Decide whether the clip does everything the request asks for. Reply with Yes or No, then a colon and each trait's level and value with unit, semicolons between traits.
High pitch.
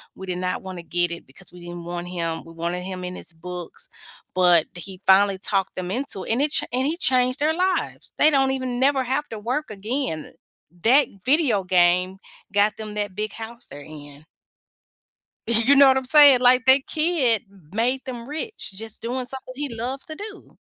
Yes: high, 225 Hz